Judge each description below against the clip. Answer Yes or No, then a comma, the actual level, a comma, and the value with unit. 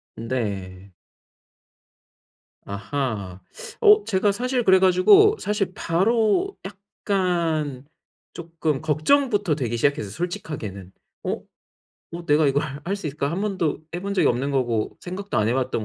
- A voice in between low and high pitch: Yes, medium, 160 Hz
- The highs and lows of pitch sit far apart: Yes, wide, 7.8 semitones